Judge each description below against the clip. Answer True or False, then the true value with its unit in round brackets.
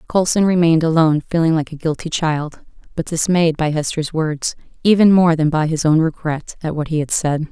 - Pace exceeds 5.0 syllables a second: True (5.4 syllables/s)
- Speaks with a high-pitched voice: False (160 Hz)